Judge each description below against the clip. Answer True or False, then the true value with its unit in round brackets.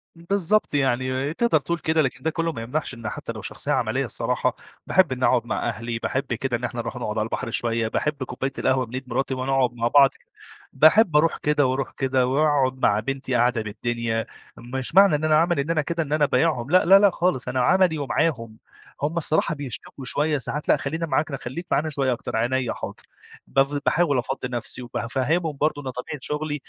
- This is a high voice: False (135 Hz)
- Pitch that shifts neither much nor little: True (3.8 semitones)